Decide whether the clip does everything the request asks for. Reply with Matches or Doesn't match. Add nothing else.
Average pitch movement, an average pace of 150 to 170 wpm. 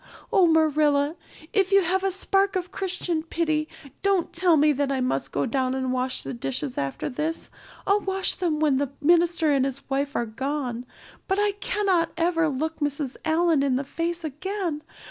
Doesn't match